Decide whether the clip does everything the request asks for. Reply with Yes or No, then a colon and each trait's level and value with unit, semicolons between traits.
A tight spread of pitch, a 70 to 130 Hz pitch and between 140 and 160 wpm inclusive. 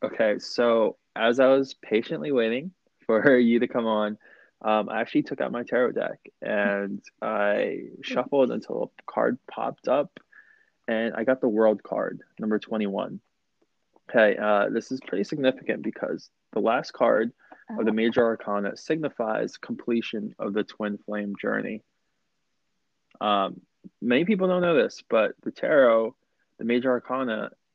No: average, 3.4 semitones; low, 115 Hz; average, 150 wpm